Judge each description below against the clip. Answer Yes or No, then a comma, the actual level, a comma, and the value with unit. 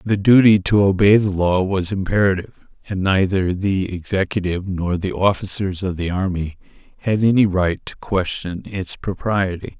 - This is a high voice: No, very low, 95 Hz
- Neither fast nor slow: Yes, average, 155 wpm